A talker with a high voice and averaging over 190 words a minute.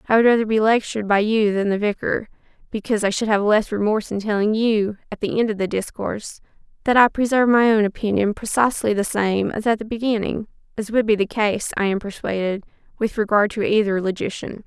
Yes: high, 210 Hz; fast, 205 wpm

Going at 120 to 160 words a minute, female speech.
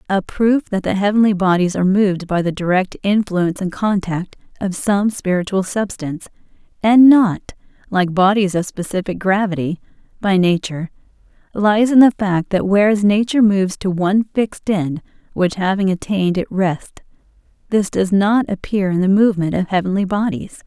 Yes: average, 155 wpm; female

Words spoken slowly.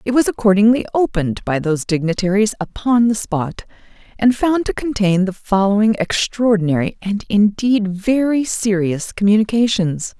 Yes: slow, 130 wpm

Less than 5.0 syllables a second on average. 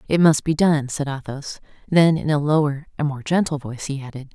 No: 5.5 syllables/s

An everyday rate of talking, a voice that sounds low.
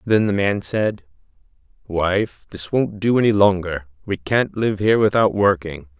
Yes: average, 160 wpm; low, 100 Hz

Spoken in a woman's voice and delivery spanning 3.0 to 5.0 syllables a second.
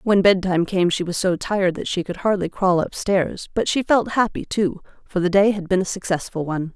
No: female; 5.5 syllables/s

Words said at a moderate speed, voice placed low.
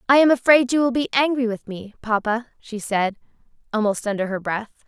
No: average, 195 wpm; high, 230 Hz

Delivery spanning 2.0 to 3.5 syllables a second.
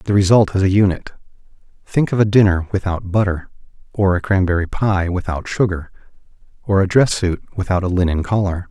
No: 5.6 syllables/s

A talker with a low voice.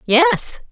No: very high, 305 Hz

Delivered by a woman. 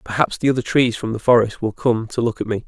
No: male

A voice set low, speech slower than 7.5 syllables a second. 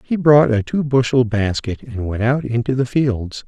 Yes: low, 125 Hz; 4.5 syllables/s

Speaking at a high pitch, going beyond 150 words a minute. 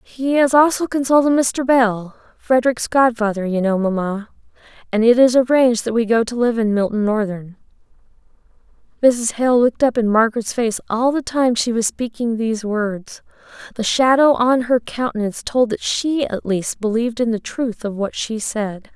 Yes: high, 235 Hz; average, 175 wpm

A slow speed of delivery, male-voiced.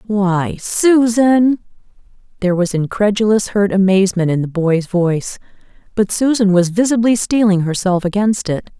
No: slow, 130 wpm; female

